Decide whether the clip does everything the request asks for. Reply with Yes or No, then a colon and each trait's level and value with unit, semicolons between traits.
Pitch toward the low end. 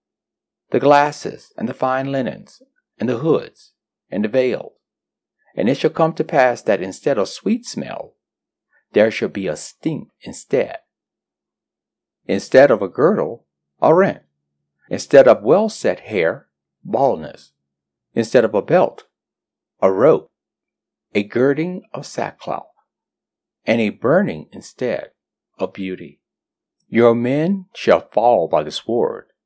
Yes: low, 120 Hz